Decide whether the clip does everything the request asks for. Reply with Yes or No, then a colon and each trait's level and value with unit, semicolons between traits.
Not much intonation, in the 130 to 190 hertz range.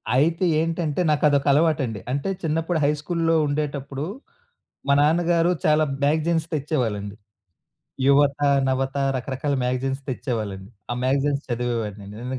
No: average, 3.5 semitones; medium, 140 Hz